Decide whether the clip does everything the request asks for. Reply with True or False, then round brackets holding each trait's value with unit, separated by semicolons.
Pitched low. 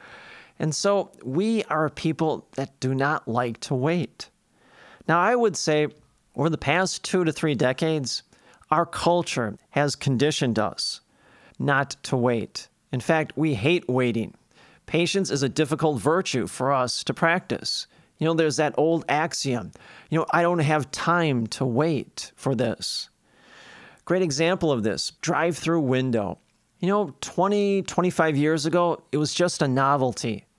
False (155 Hz)